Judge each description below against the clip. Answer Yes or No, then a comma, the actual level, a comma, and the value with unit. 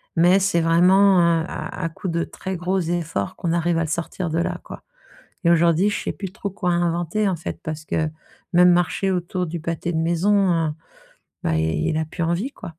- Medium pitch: Yes, medium, 170 Hz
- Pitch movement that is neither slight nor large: No, narrow, 2.1 semitones